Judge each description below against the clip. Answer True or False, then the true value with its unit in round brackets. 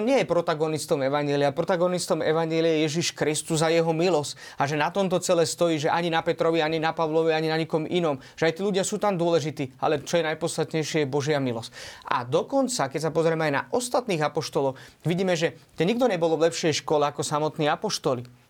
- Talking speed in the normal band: False (205 wpm)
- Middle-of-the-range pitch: True (160 Hz)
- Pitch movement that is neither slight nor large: False (2.1 semitones)